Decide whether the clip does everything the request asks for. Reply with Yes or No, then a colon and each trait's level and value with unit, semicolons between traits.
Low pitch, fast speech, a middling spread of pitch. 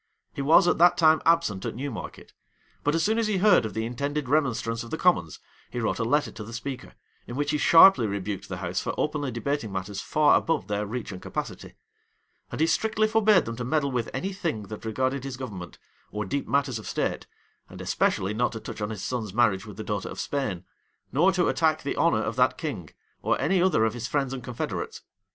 No: low, 130 Hz; fast, 225 wpm; wide, 6.2 semitones